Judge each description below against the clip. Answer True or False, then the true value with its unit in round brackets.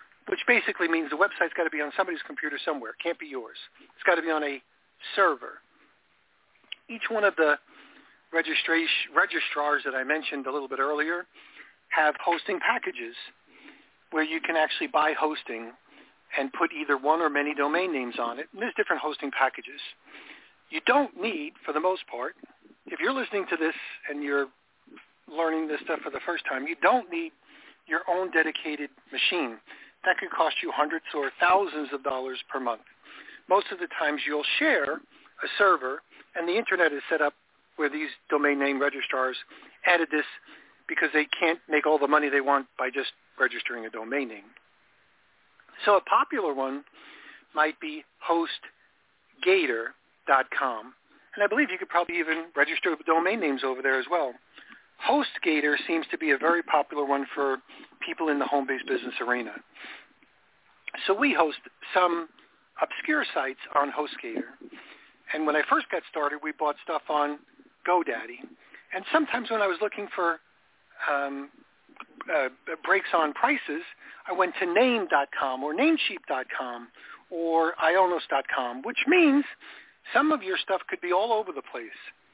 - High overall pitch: False (160 Hz)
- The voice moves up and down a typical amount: False (5.7 semitones)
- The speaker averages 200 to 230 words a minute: False (160 wpm)